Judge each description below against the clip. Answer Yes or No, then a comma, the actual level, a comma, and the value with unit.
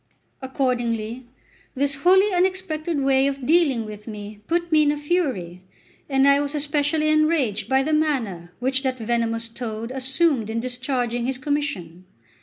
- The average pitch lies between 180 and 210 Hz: No, very high, 265 Hz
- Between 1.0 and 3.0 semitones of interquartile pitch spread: No, average, 4.7 semitones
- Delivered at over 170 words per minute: No, average, 150 wpm